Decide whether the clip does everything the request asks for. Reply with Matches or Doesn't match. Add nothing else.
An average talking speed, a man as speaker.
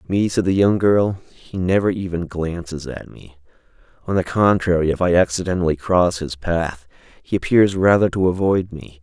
Matches